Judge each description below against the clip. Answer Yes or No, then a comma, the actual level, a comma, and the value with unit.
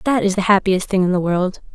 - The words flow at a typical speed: No, fast, 275 wpm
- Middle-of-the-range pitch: No, high, 195 Hz